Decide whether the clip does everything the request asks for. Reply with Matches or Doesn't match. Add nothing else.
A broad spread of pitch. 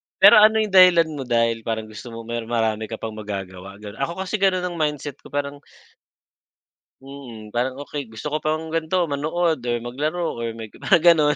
Matches